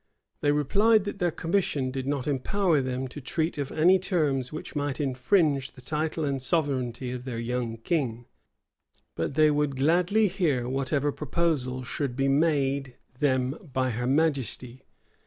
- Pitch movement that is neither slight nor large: Yes, average, 3.6 semitones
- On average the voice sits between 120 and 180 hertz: Yes, medium, 140 Hz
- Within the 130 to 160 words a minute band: Yes, average, 155 wpm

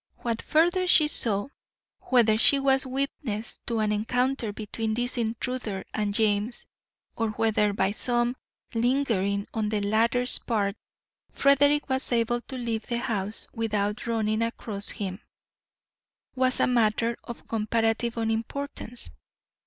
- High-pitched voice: Yes, high, 230 Hz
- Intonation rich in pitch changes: No, average, 2.8 semitones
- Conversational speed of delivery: No, slow, 130 wpm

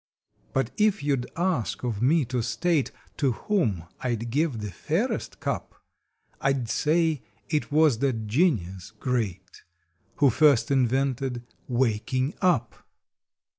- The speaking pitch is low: Yes, low, 130 Hz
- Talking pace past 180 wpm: No, slow, 135 wpm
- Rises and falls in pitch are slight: No, average, 4.5 semitones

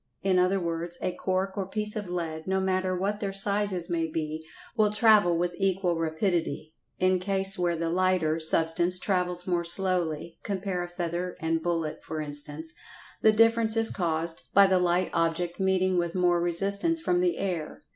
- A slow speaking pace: No, average, 175 wpm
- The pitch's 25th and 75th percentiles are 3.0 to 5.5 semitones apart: No, narrow, 2.6 semitones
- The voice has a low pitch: No, medium, 180 Hz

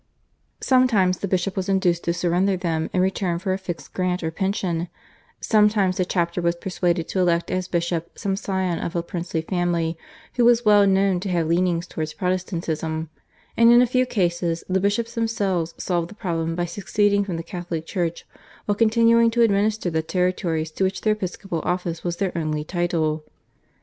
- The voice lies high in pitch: No, medium, 180 Hz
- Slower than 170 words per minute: No, average, 180 wpm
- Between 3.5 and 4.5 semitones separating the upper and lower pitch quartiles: No, average, 2.7 semitones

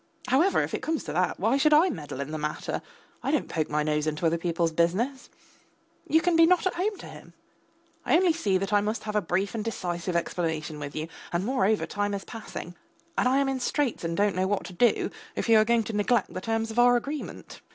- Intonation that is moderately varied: No, wide, 6.9 semitones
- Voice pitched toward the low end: No, high, 205 Hz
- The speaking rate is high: Yes, fast, 240 wpm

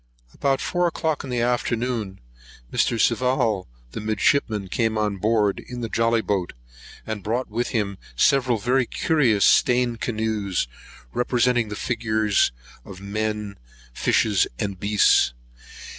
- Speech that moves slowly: Yes, slow, 130 wpm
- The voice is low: Yes, low, 110 Hz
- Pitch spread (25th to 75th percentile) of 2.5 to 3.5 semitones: Yes, average, 2.9 semitones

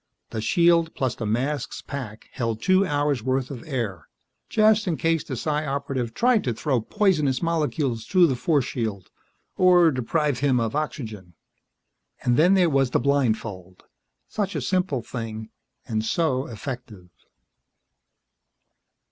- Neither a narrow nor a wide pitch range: No, wide, 6.0 semitones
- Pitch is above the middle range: No, low, 135 Hz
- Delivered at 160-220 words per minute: No, average, 140 wpm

